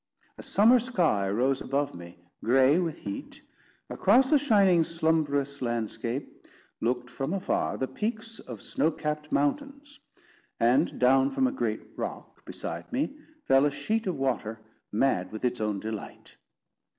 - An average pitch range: No, wide, 8.3 semitones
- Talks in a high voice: No, medium, 140 Hz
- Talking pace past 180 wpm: No, average, 145 wpm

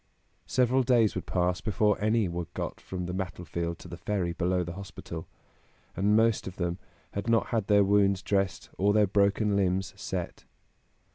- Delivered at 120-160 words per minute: No, average, 170 wpm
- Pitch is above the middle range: No, low, 100 Hz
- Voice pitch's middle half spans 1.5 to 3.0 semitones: Yes, narrow, 2.6 semitones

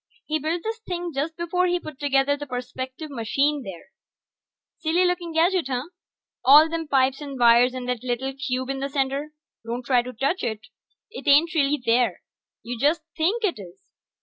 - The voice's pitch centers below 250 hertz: No, very high, 280 Hz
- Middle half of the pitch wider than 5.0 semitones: No, average, 4.4 semitones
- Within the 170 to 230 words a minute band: Yes, average, 180 wpm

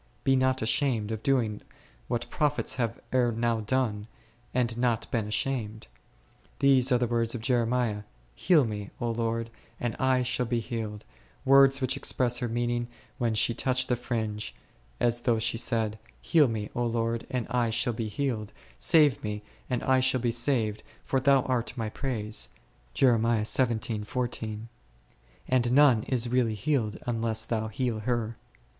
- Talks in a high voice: No, low, 120 Hz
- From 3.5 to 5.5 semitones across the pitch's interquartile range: No, narrow, 2.5 semitones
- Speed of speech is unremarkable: Yes, average, 150 wpm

